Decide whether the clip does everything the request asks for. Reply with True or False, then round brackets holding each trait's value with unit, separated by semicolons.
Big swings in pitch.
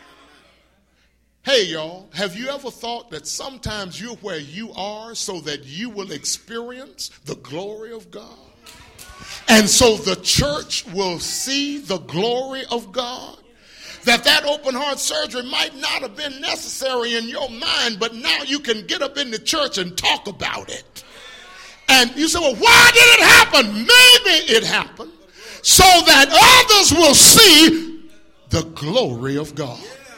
True (6.9 semitones)